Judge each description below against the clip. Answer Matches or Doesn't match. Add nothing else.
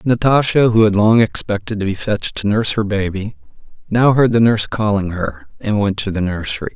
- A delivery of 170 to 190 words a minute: Doesn't match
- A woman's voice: Doesn't match